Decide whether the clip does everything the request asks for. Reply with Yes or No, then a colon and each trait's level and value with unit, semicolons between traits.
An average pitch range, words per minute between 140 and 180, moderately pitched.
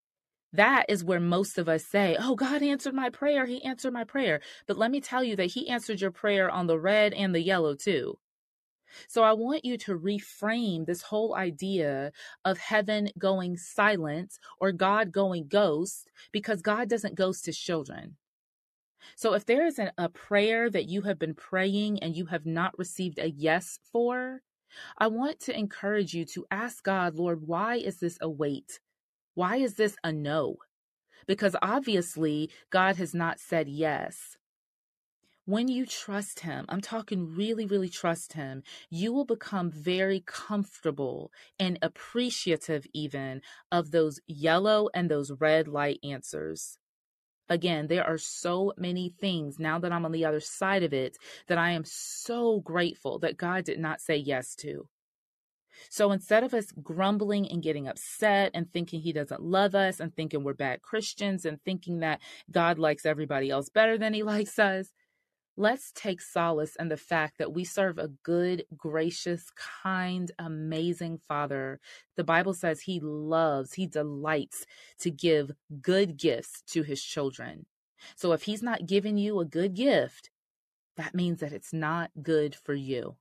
Yes: average, 4.6 semitones; average, 165 wpm; medium, 180 Hz